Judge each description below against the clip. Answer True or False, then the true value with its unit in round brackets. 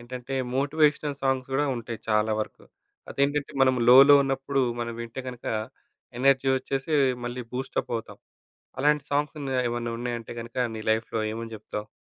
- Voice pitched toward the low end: True (130 Hz)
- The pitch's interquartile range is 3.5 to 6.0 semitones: False (2.8 semitones)